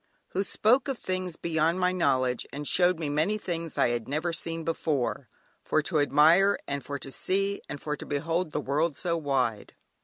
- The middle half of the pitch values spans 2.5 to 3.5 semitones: No, average, 4.2 semitones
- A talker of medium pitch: Yes, medium, 160 Hz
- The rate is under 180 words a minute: No, average, 190 wpm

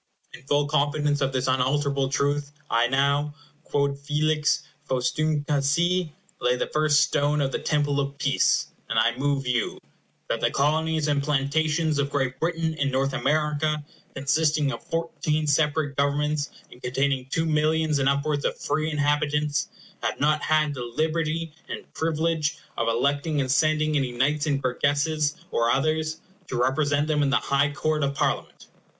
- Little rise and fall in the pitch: Yes, narrow, 1.8 semitones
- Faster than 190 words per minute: No, average, 160 wpm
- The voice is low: No, medium, 145 Hz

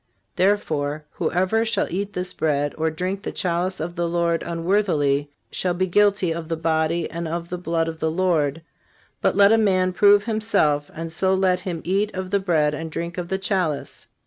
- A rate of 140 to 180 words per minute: No, average, 200 wpm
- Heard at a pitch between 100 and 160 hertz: No, medium, 175 Hz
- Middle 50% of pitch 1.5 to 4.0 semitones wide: Yes, average, 2.9 semitones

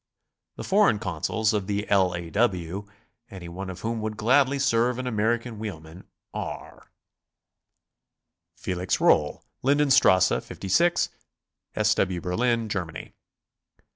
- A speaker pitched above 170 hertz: No, low, 105 Hz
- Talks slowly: Yes, slow, 120 wpm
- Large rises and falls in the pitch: No, average, 4.4 semitones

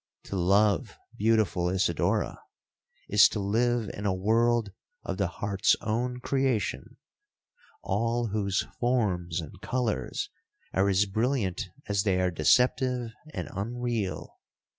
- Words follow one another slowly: Yes, slow, 115 wpm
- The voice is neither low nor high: No, low, 105 Hz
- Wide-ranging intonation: No, average, 3.9 semitones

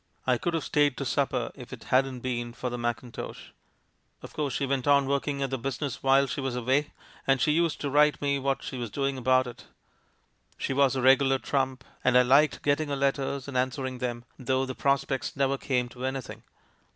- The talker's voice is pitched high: No, low, 135 Hz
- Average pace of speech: No, fast, 210 wpm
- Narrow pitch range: Yes, narrow, 1.6 semitones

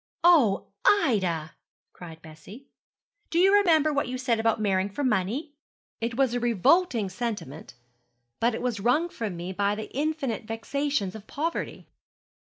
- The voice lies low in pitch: No, high, 230 Hz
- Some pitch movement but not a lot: No, wide, 6.3 semitones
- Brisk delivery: No, average, 150 wpm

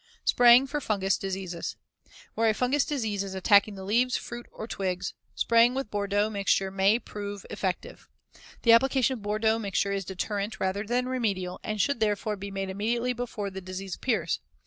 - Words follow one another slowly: No, average, 170 wpm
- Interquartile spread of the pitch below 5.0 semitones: Yes, average, 3.4 semitones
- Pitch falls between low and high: No, high, 205 Hz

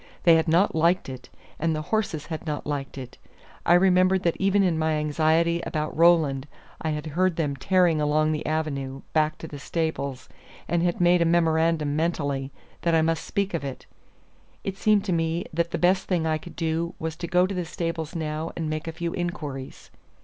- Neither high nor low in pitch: Yes, medium, 160 Hz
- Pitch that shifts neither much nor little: No, narrow, 2.2 semitones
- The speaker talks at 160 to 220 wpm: Yes, average, 200 wpm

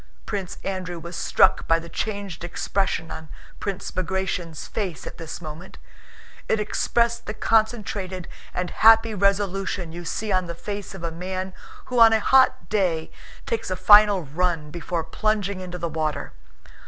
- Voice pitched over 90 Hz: Yes, medium, 185 Hz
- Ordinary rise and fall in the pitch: Yes, average, 3.4 semitones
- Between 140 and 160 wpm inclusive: Yes, average, 155 wpm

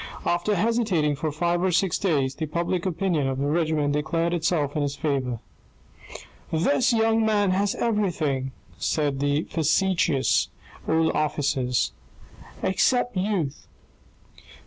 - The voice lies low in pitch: No, medium, 160 Hz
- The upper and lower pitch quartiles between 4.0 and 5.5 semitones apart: Yes, average, 4.7 semitones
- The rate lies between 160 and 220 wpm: No, average, 140 wpm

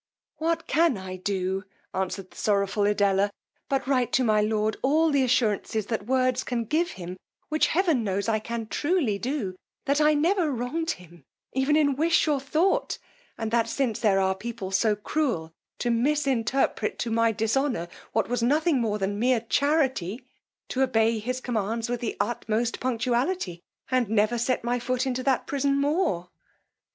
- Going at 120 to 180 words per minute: Yes, average, 165 wpm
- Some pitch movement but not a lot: Yes, average, 4.8 semitones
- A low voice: No, high, 240 Hz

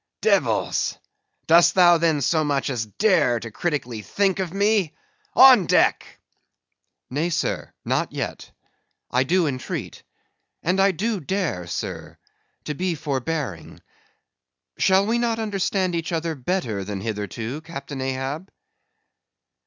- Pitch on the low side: No, medium, 165 Hz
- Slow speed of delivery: Yes, slow, 120 wpm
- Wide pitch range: Yes, wide, 6.4 semitones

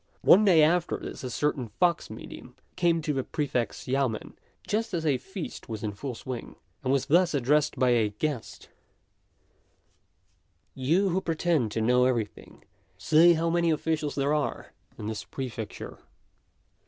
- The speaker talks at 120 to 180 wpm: Yes, average, 155 wpm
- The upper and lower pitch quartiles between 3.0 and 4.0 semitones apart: No, average, 5.0 semitones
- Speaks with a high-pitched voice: No, medium, 145 Hz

